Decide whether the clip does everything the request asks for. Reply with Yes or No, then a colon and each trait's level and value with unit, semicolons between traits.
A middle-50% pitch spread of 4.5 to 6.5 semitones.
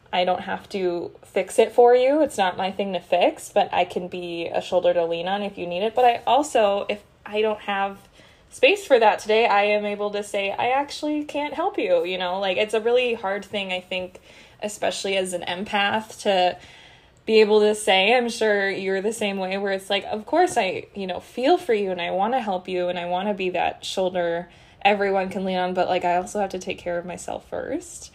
No: average, 3.3 semitones